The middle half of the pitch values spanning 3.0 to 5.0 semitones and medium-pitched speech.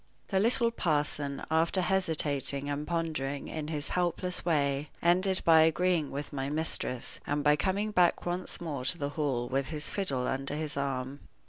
Yes: average, 3.8 semitones; medium, 150 Hz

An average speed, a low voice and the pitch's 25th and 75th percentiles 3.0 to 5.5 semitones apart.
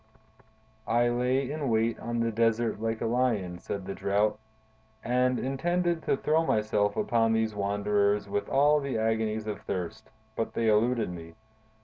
Yes: average, 155 wpm; low, 115 Hz; average, 3.3 semitones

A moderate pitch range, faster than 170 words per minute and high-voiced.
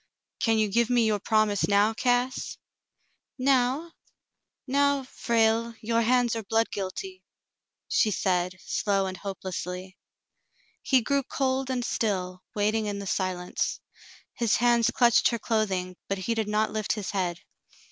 No: average, 3.7 semitones; average, 145 wpm; high, 220 Hz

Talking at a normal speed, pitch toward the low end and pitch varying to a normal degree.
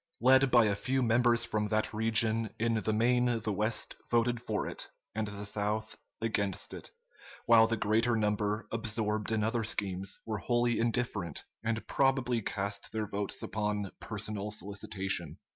No: average, 155 wpm; low, 110 Hz; narrow, 2.0 semitones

